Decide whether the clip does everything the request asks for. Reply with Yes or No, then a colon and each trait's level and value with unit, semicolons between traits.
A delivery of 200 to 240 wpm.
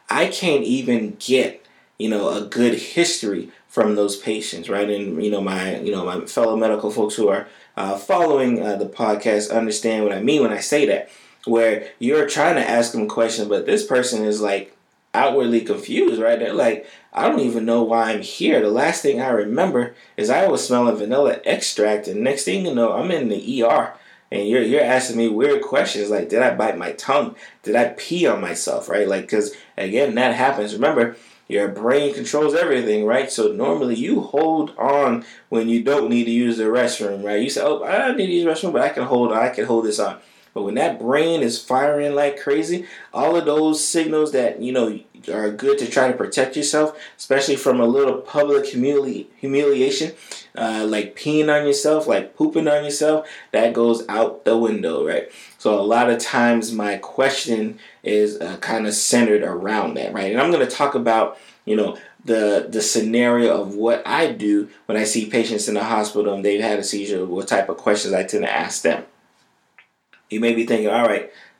Yes: fast, 205 wpm